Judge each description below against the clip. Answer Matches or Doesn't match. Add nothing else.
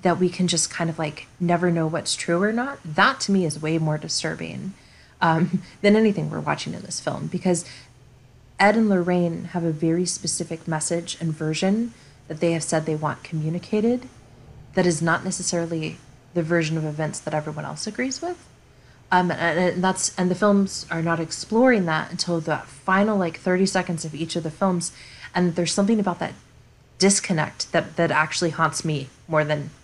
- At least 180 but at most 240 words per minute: Matches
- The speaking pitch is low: Doesn't match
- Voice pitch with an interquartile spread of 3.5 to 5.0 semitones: Doesn't match